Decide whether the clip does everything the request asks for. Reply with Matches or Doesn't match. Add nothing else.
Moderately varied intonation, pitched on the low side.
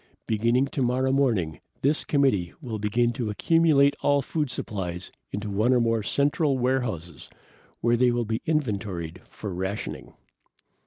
Matches